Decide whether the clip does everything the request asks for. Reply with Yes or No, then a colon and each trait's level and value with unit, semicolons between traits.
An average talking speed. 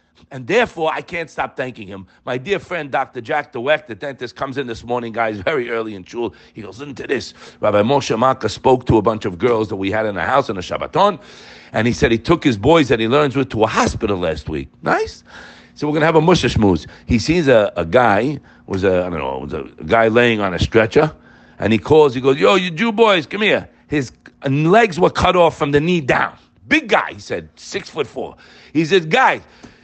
No: fast, 240 wpm